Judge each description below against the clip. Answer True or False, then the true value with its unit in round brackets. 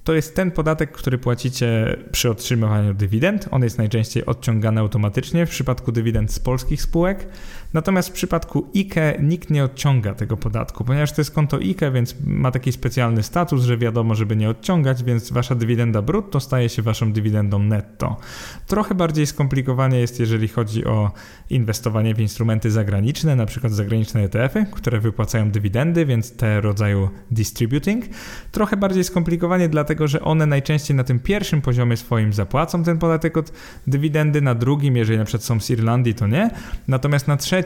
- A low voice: True (125 Hz)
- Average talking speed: False (165 wpm)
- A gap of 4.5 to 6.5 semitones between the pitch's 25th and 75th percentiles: True (5.6 semitones)